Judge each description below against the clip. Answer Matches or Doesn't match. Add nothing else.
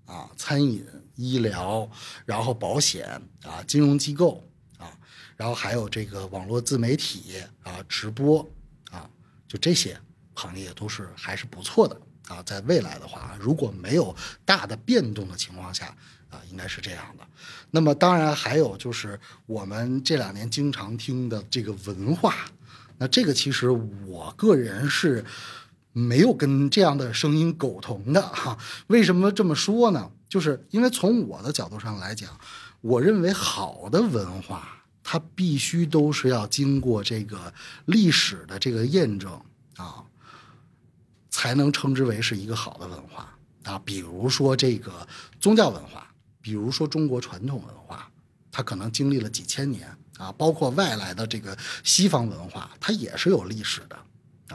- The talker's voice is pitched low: Matches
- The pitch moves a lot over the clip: Matches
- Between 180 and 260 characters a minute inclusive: Matches